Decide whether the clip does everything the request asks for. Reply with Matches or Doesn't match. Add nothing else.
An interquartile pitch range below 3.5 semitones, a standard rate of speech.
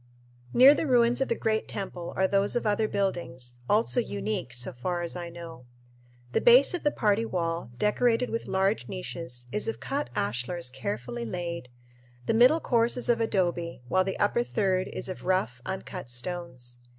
Doesn't match